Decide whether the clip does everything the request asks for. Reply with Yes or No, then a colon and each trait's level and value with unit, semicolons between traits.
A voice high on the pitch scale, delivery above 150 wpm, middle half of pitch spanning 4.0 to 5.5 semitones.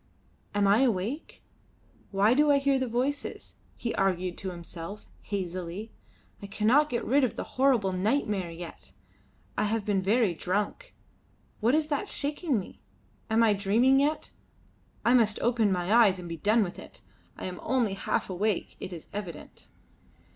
Yes: high, 210 Hz; average, 160 wpm; average, 5.1 semitones